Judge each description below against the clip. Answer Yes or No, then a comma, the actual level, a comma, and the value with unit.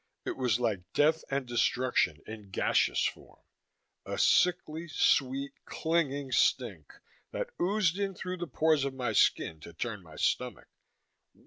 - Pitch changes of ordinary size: No, wide, 6.5 semitones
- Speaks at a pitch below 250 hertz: Yes, low, 135 Hz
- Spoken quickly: No, average, 140 wpm